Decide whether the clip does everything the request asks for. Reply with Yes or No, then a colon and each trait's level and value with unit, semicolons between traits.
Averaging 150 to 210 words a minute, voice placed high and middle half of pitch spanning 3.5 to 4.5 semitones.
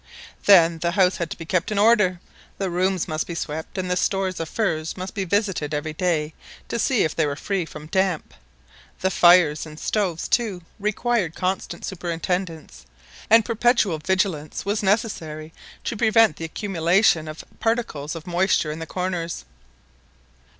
No: average, 165 wpm; medium, 180 Hz; average, 3.9 semitones